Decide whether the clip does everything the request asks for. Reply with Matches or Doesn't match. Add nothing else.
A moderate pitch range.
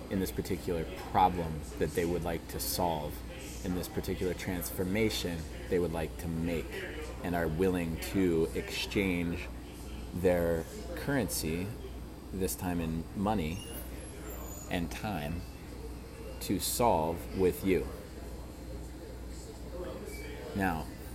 Matches